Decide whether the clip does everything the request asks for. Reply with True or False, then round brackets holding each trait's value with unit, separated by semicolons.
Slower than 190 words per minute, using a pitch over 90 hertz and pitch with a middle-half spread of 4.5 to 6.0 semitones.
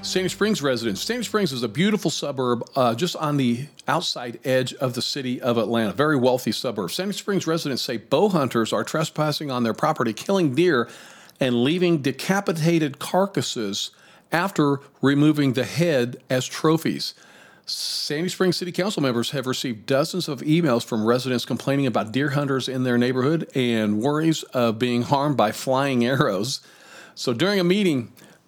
True (165 wpm; 140 Hz; 5.0 semitones)